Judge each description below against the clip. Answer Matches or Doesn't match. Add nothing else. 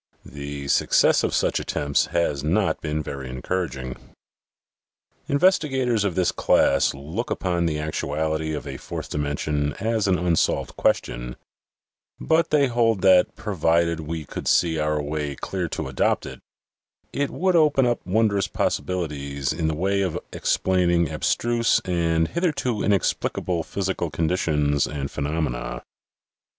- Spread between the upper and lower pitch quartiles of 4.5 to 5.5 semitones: Matches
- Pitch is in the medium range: Doesn't match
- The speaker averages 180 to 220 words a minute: Doesn't match